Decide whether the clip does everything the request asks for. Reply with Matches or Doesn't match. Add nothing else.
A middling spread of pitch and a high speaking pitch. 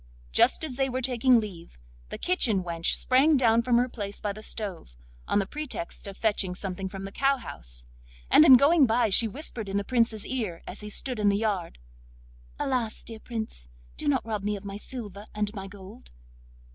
Matches